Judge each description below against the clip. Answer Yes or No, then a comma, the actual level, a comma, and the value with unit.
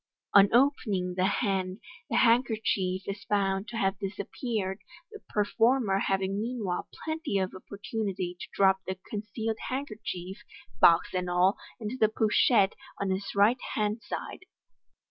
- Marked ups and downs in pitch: No, average, 2.8 semitones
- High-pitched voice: Yes, high, 200 Hz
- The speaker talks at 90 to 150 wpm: Yes, average, 140 wpm